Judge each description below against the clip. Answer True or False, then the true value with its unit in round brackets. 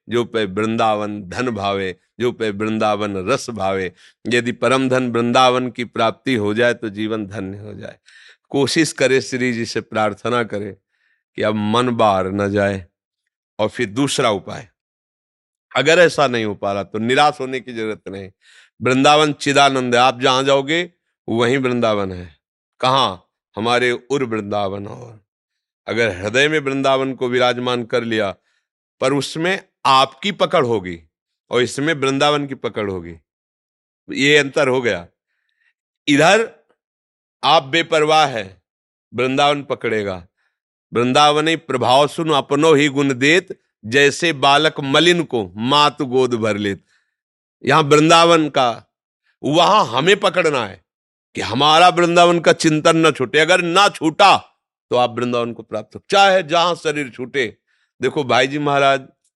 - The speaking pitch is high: False (125 Hz)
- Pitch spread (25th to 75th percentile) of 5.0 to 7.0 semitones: True (5.4 semitones)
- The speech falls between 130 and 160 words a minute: True (145 wpm)